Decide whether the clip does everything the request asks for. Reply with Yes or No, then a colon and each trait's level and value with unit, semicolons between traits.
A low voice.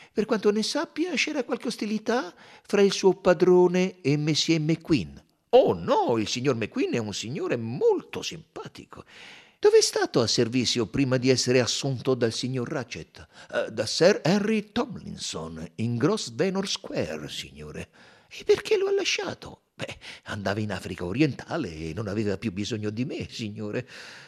No: medium, 150 Hz